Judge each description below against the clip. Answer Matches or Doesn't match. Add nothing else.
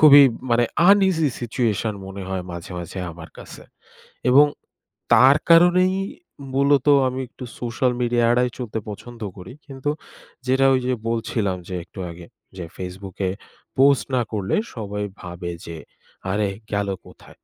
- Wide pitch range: Matches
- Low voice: Matches